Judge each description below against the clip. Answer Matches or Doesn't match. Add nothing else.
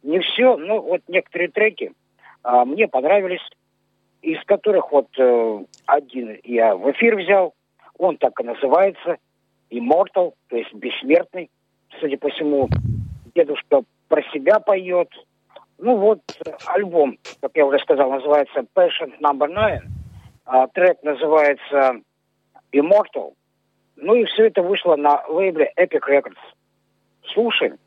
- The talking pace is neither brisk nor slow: Matches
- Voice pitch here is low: Doesn't match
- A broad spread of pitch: Matches